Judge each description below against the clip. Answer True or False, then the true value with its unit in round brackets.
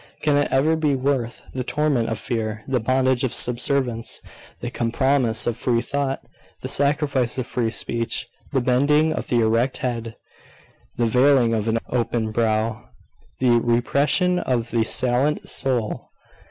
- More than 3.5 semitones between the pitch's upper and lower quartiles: False (3.1 semitones)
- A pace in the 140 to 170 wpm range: True (150 wpm)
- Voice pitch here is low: True (125 Hz)